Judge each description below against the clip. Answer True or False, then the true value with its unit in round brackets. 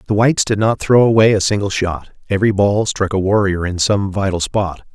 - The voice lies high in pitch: False (100 Hz)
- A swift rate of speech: True (220 wpm)